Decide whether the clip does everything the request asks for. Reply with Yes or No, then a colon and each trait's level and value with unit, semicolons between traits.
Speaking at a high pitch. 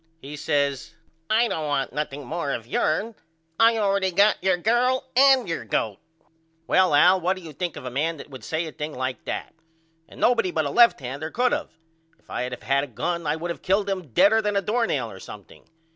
No: medium, 165 Hz